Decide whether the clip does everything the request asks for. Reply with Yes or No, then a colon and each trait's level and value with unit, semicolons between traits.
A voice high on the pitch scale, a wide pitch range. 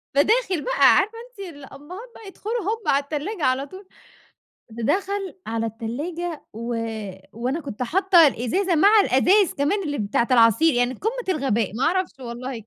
Yes: very high, 300 Hz; wide, 7.7 semitones